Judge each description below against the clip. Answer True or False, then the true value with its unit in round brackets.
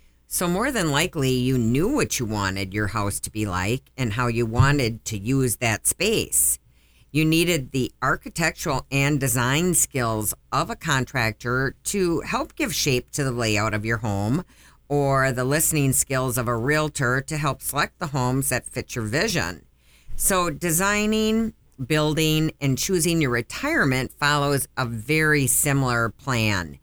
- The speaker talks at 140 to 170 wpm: True (155 wpm)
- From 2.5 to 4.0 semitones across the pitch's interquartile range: False (4.8 semitones)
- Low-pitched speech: True (130 Hz)